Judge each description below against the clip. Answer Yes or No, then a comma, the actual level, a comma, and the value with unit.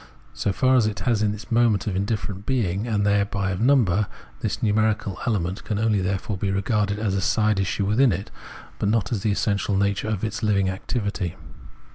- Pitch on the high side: No, low, 105 Hz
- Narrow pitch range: Yes, narrow, 2.0 semitones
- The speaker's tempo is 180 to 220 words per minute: Yes, average, 200 wpm